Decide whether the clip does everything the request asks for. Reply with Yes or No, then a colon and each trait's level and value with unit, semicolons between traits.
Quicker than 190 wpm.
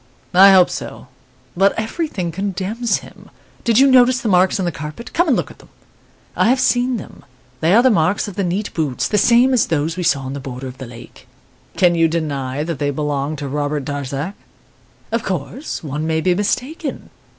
Yes: fast, 205 wpm